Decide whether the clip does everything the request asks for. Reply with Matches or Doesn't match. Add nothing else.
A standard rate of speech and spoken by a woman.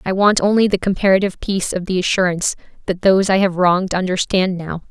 Matches